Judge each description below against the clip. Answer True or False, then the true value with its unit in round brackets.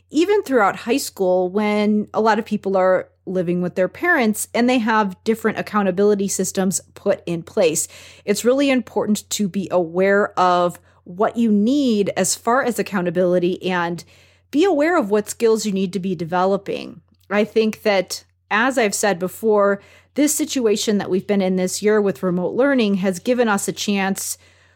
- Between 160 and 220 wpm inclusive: True (170 wpm)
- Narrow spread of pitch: False (3.3 semitones)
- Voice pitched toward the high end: True (200 Hz)